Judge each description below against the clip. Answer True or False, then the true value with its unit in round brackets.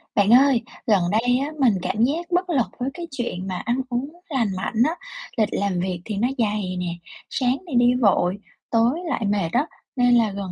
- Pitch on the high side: True (235 Hz)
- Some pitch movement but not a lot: True (4.6 semitones)